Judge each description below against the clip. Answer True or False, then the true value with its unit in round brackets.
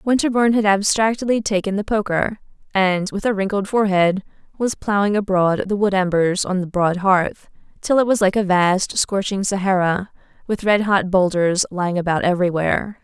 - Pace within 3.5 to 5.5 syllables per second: True (5.2 syllables/s)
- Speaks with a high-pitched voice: True (195 Hz)